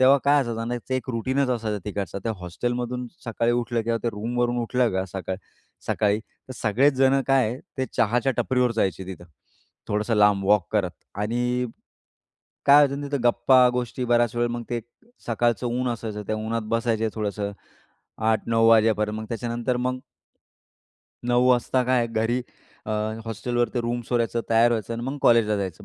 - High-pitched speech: No, low, 115 Hz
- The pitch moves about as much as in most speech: No, narrow, 2.3 semitones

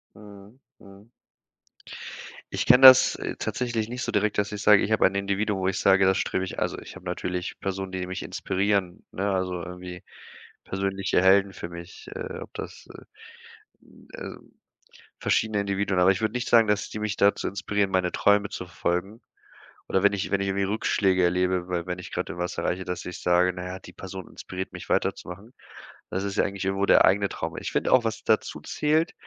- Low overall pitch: Yes, very low, 95 Hz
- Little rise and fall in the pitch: Yes, narrow, 2.0 semitones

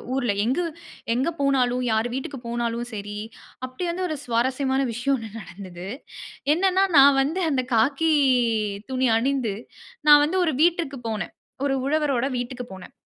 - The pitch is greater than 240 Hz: Yes, very high, 265 Hz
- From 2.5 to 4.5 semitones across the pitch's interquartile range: Yes, average, 3.7 semitones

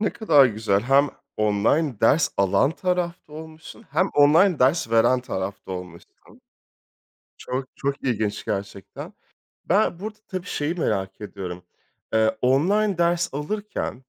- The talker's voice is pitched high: No, low, 135 Hz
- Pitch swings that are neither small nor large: No, wide, 8.2 semitones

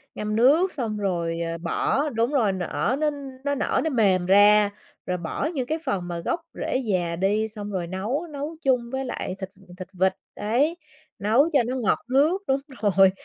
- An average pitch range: No, wide, 6.5 semitones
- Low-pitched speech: No, high, 215 Hz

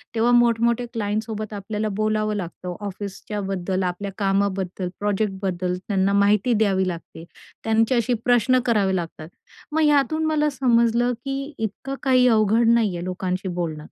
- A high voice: Yes, high, 210 Hz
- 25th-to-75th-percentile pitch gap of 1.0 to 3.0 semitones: No, average, 3.7 semitones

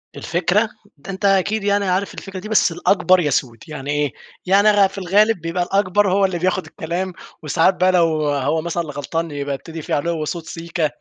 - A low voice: No, medium, 175 Hz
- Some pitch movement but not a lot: Yes, average, 3.5 semitones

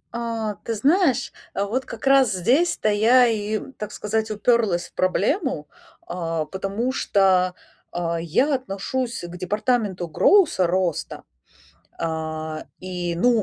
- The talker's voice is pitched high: Yes, high, 205 Hz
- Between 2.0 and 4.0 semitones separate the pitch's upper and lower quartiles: No, wide, 5.6 semitones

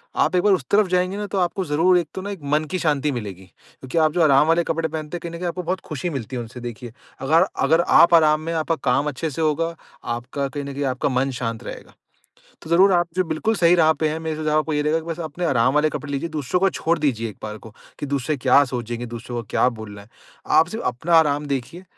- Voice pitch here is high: No, medium, 155 Hz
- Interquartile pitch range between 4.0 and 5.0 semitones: Yes, average, 4.3 semitones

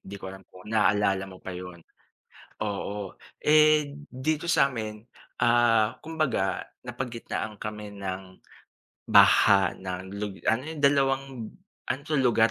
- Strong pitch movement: Yes, wide, 5.7 semitones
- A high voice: No, low, 110 Hz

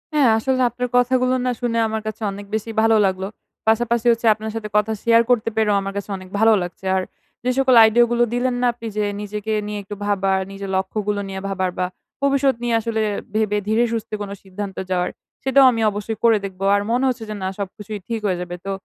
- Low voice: No, high, 220 Hz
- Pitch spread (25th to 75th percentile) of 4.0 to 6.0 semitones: No, average, 3.1 semitones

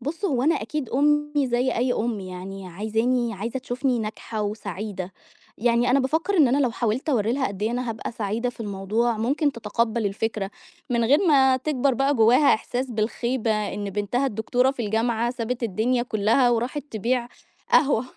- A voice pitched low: No, high, 240 Hz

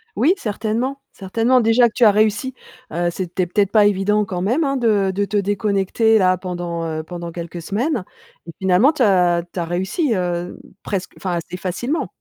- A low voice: No, high, 195 Hz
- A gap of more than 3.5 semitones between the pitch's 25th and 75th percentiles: Yes, average, 4.0 semitones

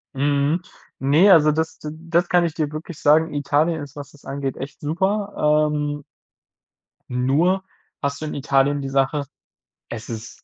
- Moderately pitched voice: Yes, medium, 150 Hz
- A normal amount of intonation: No, narrow, 2.3 semitones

